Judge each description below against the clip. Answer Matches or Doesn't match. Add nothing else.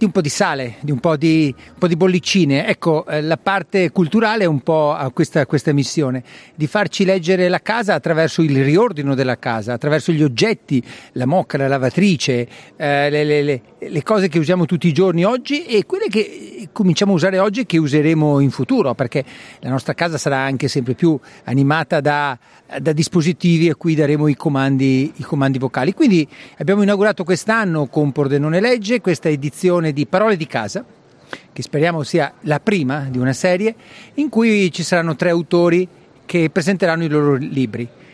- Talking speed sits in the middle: Doesn't match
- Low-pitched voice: Doesn't match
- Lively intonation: Doesn't match